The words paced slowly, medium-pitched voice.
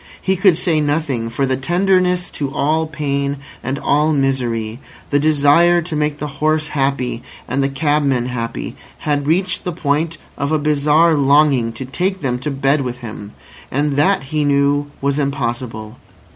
No: average, 165 wpm; medium, 145 Hz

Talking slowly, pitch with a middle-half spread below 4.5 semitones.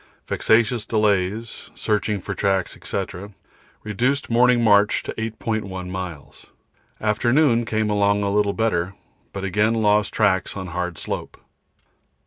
Yes: slow, 120 wpm; narrow, 2.4 semitones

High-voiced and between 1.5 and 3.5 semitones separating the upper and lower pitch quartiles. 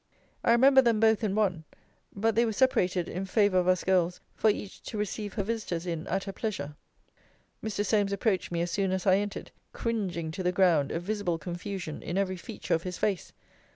Yes: high, 195 Hz; average, 3.2 semitones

